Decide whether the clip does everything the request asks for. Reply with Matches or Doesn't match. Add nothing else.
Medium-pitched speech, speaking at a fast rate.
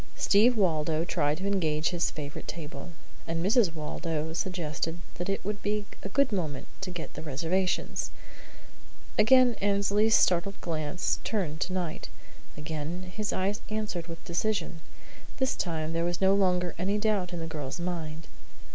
Doesn't match